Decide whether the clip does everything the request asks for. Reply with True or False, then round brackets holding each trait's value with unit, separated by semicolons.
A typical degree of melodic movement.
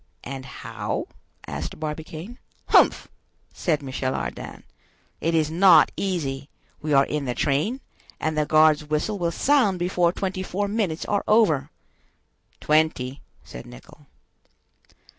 True (4.8 semitones)